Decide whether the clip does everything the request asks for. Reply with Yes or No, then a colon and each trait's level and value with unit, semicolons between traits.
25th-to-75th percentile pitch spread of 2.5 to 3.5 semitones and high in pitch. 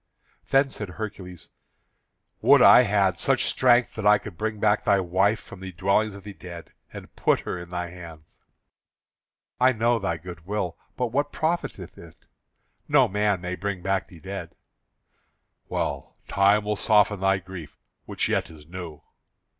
No: average, 3.0 semitones; very low, 95 Hz